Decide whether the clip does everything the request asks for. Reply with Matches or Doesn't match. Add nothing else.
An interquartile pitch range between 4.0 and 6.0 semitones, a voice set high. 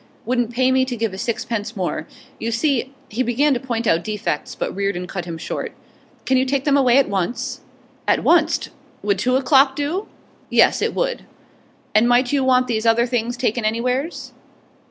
Doesn't match